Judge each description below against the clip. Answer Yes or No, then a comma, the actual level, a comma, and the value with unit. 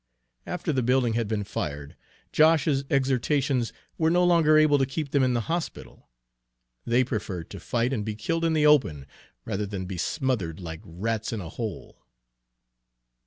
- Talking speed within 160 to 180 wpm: Yes, average, 170 wpm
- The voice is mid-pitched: No, low, 125 Hz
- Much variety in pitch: Yes, wide, 6.4 semitones